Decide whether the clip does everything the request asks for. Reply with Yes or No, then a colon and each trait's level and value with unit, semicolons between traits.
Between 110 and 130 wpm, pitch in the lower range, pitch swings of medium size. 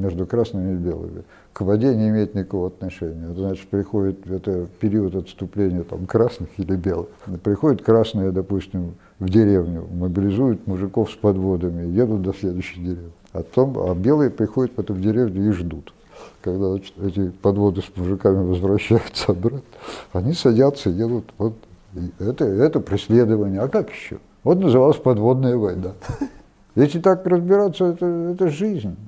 No: average, 150 wpm; low, 100 Hz; average, 4.1 semitones